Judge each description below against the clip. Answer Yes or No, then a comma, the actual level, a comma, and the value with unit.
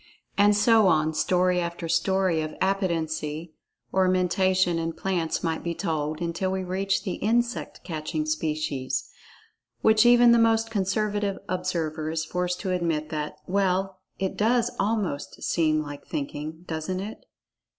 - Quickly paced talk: No, average, 140 wpm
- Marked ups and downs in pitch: No, average, 3.6 semitones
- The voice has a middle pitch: Yes, medium, 180 Hz